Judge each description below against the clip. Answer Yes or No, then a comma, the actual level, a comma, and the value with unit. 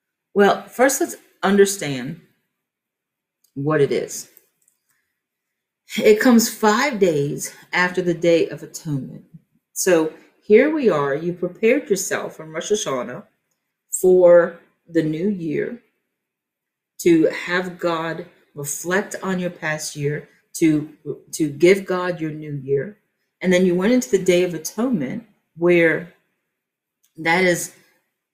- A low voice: No, medium, 180 Hz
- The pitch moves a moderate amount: Yes, average, 4.4 semitones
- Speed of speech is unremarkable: No, slow, 120 wpm